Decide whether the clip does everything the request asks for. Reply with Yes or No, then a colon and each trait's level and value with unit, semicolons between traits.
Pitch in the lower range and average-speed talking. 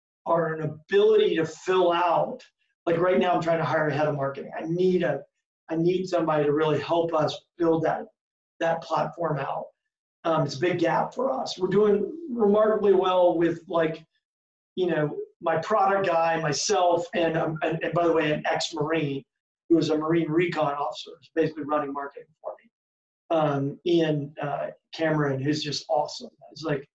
No: medium, 165 Hz; average, 180 wpm